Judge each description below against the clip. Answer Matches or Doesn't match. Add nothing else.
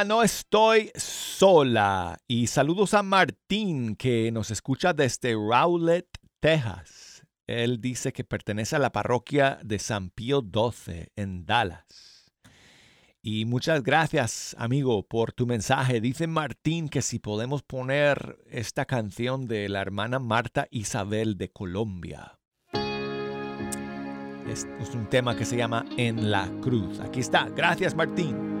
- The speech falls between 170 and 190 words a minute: Doesn't match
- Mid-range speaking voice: Doesn't match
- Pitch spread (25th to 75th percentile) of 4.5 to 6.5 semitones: Matches